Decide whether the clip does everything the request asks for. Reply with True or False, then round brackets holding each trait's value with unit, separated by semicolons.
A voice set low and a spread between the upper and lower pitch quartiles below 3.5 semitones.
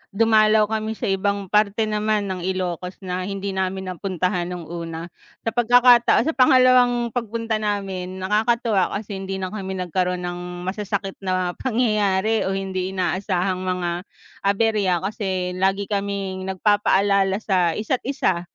False (195 Hz; 2.6 semitones)